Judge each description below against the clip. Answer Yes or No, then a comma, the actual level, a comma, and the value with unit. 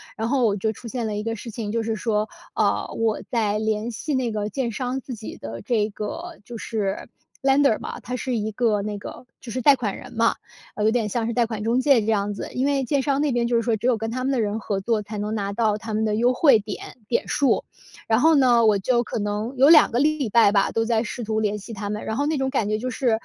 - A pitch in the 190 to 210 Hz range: No, high, 225 Hz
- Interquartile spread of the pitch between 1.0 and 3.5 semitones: Yes, average, 3.0 semitones